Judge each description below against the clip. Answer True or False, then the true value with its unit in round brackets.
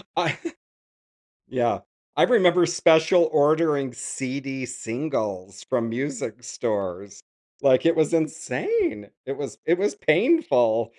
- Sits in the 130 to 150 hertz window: True (140 Hz)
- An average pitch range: False (6.1 semitones)